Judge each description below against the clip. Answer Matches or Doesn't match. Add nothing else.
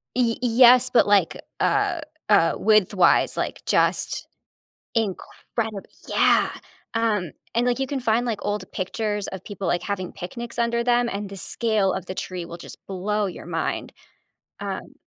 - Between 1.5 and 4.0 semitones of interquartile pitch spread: Matches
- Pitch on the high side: Matches